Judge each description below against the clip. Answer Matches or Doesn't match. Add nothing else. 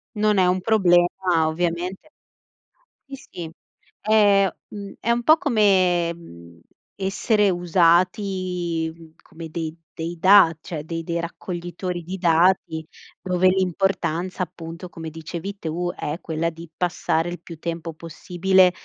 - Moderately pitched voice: Matches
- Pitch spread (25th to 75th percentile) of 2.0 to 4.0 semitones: Matches